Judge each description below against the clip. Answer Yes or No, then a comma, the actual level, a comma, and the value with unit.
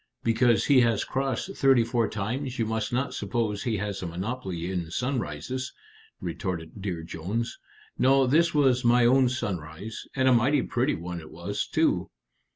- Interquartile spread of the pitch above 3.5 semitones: Yes, wide, 5.5 semitones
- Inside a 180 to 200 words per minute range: No, average, 165 wpm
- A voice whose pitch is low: Yes, low, 115 Hz